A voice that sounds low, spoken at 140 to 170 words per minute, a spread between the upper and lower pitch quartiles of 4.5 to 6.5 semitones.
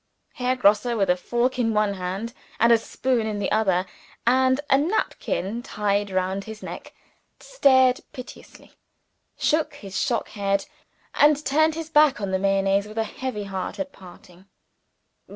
No: high, 220 Hz; average, 155 wpm; average, 4.8 semitones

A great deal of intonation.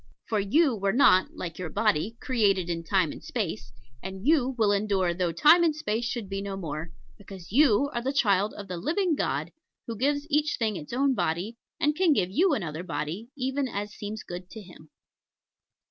Yes: wide, 6.5 semitones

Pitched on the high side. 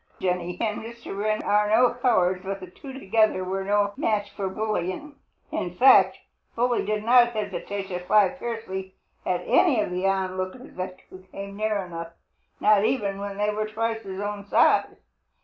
Yes: high, 205 Hz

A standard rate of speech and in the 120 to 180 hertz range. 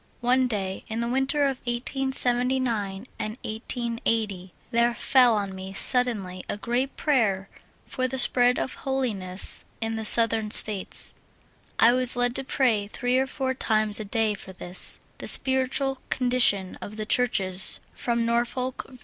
No: average, 155 wpm; high, 235 Hz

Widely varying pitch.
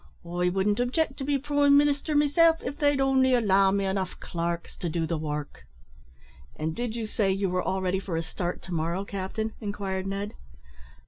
Yes: wide, 6.8 semitones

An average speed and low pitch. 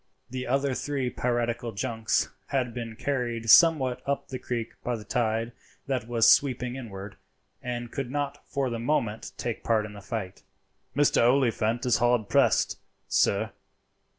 Yes: average, 150 wpm; low, 120 Hz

